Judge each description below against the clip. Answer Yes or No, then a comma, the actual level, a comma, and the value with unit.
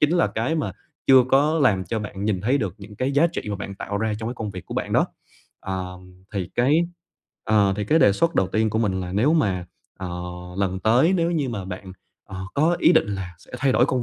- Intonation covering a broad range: Yes, wide, 6.2 semitones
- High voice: No, low, 105 Hz